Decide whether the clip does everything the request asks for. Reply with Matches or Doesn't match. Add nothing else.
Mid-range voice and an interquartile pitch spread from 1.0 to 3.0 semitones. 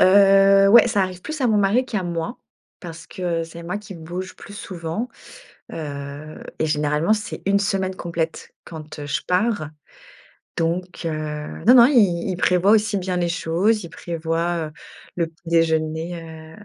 Doesn't match